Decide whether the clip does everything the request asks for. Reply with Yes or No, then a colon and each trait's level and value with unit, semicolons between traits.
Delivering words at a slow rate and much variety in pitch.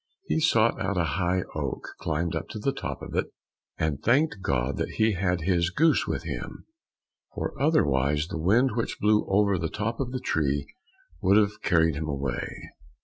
No: average, 185 wpm; wide, 5.7 semitones